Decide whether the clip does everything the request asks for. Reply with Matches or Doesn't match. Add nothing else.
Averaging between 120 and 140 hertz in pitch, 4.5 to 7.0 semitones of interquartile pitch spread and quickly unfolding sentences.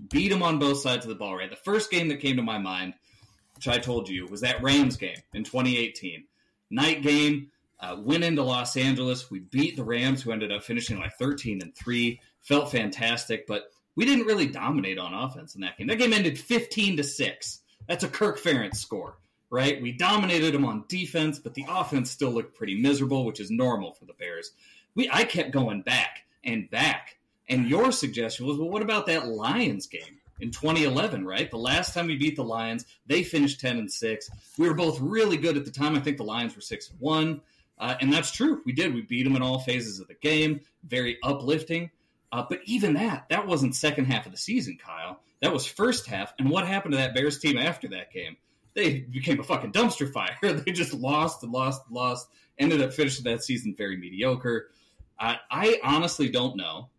Matches